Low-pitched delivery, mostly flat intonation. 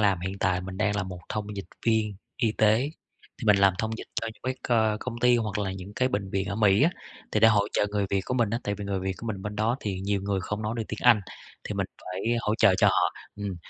Yes: low, 105 Hz; narrow, 2.3 semitones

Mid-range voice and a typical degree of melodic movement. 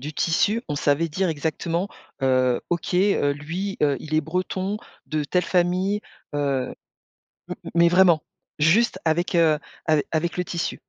Yes: medium, 165 Hz; average, 3.5 semitones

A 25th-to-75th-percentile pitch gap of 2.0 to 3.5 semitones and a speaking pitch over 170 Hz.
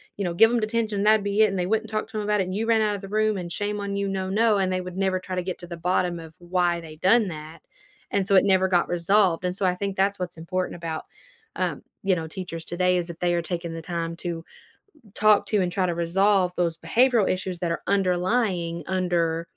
Yes: average, 2.8 semitones; medium, 185 Hz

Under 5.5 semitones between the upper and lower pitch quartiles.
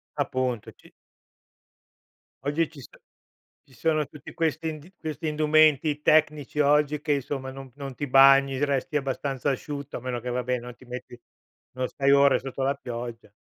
Yes: average, 2.7 semitones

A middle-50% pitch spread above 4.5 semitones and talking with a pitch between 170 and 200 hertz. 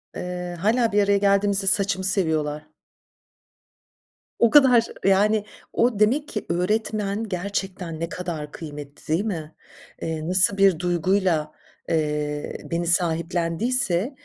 No: average, 3.9 semitones; medium, 185 Hz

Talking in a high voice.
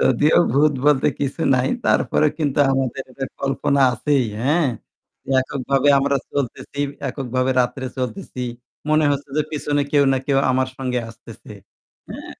No: low, 135 Hz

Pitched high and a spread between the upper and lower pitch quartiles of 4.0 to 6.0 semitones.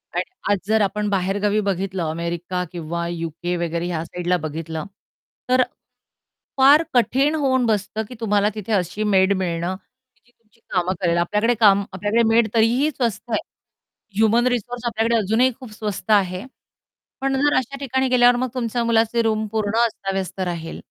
Yes: high, 210 Hz; average, 4.3 semitones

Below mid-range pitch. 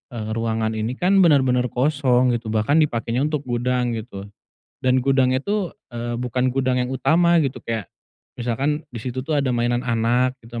Yes: low, 125 Hz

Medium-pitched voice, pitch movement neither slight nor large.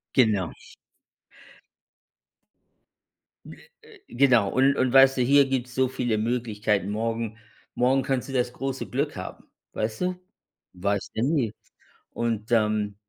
No: low, 120 Hz; average, 3.7 semitones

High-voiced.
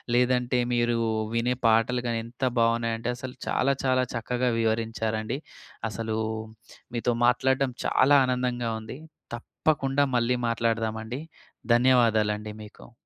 No: low, 120 Hz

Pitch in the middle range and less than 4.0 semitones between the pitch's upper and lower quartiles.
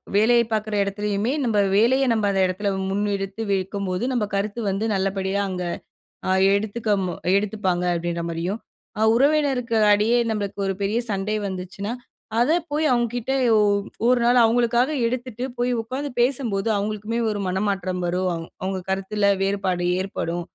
No: high, 205 Hz; average, 3.6 semitones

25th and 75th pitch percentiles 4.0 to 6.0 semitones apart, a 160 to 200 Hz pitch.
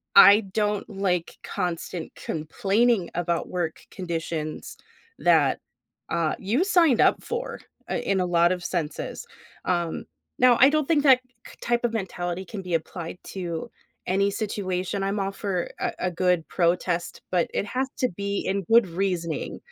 No: average, 3.5 semitones; medium, 185 Hz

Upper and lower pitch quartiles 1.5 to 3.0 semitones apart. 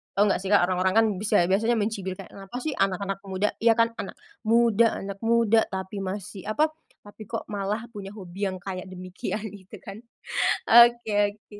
Yes: average, 2.7 semitones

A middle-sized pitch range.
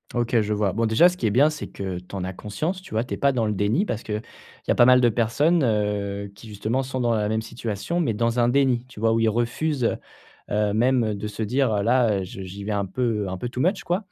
Yes: average, 3.5 semitones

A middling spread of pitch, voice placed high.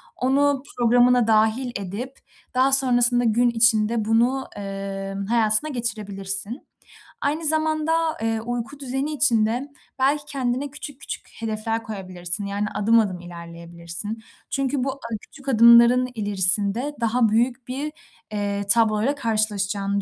Yes: average, 4.1 semitones; high, 230 Hz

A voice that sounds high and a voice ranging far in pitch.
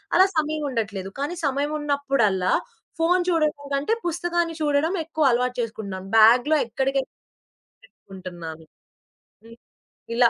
Yes: very high, 275 Hz; wide, 6.3 semitones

